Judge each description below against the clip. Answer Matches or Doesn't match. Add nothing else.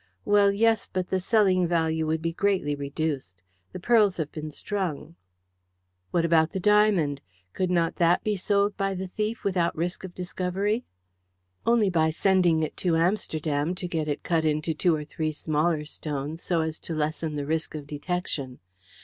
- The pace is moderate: Matches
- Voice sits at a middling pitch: Matches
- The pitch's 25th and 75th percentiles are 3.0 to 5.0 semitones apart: Matches